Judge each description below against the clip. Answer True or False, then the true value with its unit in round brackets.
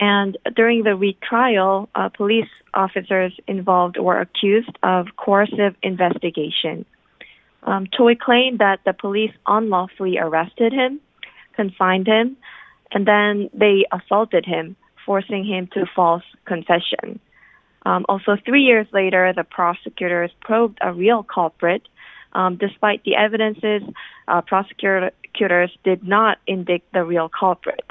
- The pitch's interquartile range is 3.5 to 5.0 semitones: False (2.9 semitones)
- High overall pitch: True (195 Hz)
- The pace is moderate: False (125 wpm)